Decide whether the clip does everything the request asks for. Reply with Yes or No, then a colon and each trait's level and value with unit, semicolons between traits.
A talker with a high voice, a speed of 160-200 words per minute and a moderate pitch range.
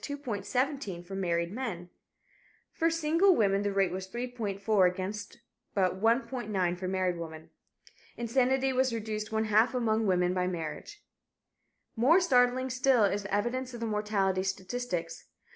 No: high, 215 Hz; average, 140 wpm; average, 4.9 semitones